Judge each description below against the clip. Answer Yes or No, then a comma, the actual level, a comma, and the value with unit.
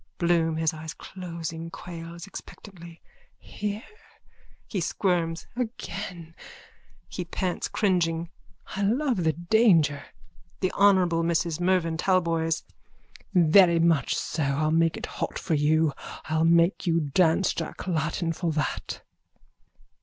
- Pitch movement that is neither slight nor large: No, narrow, 2.2 semitones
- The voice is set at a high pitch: No, medium, 170 Hz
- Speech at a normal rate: No, slow, 115 wpm